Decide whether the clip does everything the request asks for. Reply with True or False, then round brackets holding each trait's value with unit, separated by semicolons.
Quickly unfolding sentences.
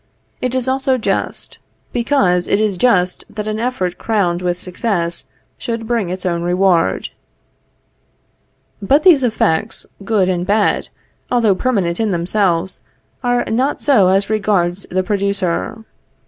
False (135 wpm)